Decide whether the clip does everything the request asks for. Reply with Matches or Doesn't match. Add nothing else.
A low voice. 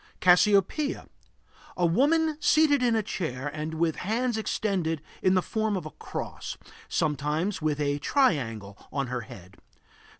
Doesn't match